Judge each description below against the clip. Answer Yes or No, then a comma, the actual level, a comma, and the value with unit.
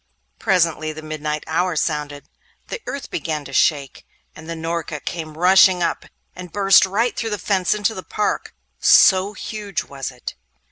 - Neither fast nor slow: Yes, average, 160 wpm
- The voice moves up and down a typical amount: Yes, average, 4.1 semitones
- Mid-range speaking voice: Yes, medium, 170 Hz